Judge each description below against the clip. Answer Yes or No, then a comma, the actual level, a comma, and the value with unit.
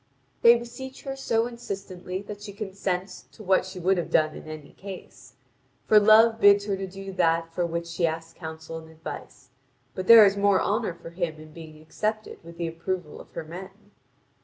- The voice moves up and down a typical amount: Yes, average, 3.7 semitones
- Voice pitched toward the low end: No, medium, 185 Hz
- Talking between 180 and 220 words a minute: Yes, average, 190 wpm